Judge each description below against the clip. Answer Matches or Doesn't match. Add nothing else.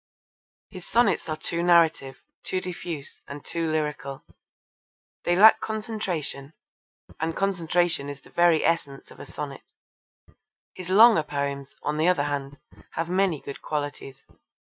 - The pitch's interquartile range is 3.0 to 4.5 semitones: Matches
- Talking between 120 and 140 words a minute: Matches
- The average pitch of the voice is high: Doesn't match